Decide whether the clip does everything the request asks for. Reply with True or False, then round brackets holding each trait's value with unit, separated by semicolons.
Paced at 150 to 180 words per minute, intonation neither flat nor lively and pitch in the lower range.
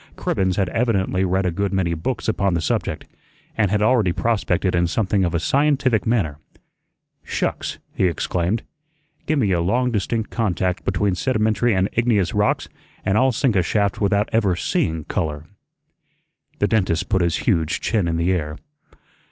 True (165 wpm; 4.1 semitones; 95 Hz)